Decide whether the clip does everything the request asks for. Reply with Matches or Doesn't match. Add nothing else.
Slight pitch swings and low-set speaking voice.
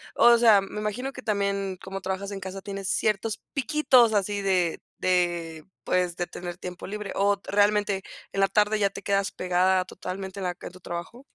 Doesn't match